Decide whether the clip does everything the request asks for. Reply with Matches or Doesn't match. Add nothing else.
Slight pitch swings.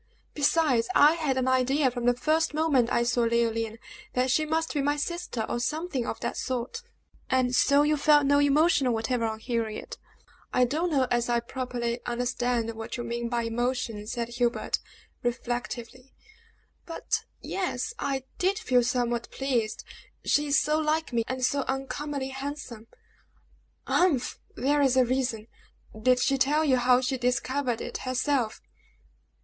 Doesn't match